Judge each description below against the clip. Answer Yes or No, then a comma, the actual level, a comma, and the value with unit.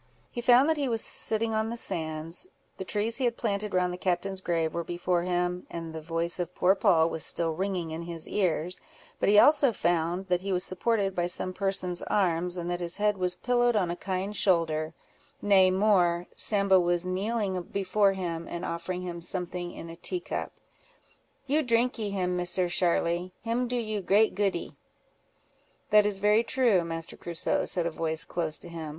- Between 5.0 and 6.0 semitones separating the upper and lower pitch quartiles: No, average, 3.3 semitones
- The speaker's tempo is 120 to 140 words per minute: No, average, 190 wpm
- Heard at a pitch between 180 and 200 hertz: Yes, medium, 185 Hz